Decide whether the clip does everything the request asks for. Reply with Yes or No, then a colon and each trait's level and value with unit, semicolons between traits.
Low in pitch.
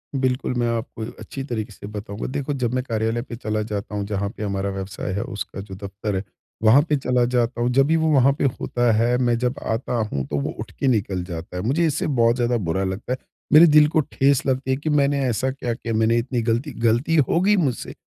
Yes: low, 120 Hz